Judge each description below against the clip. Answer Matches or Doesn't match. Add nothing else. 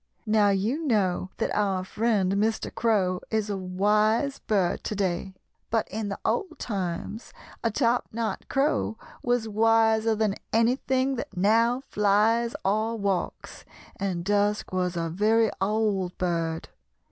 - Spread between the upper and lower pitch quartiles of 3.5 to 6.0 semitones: Doesn't match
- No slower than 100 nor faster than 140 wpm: Matches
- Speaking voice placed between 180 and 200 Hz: Doesn't match